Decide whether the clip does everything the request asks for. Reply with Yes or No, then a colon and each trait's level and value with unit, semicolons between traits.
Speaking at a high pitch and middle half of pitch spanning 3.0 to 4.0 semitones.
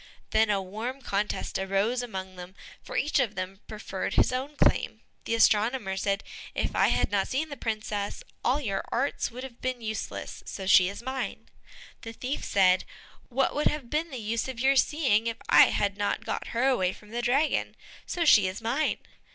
No: high, 225 Hz; average, 4.7 semitones